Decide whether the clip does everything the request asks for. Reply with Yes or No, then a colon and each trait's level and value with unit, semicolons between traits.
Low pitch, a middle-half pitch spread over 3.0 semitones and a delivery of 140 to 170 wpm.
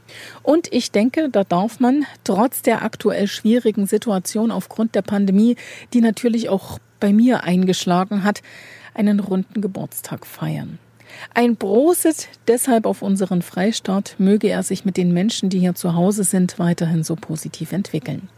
No: high, 205 Hz; average, 3.6 semitones; average, 150 wpm